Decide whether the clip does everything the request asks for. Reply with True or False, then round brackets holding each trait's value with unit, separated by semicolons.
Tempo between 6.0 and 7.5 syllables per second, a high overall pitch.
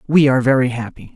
False (7.1 syllables/s; 130 Hz)